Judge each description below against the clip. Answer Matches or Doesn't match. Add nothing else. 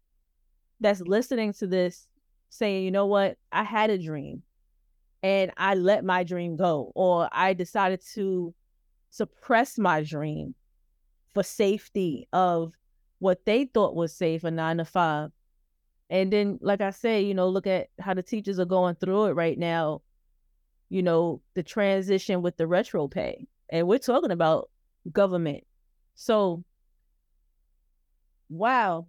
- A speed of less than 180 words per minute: Matches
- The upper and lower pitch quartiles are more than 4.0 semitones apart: Matches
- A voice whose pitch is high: Doesn't match